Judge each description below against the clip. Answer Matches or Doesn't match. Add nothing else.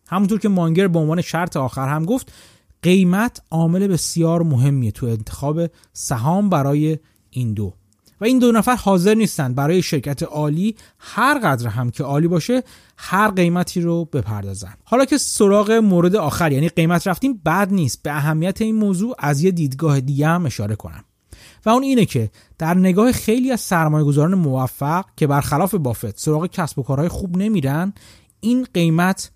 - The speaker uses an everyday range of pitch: Doesn't match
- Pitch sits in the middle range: Matches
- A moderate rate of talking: Doesn't match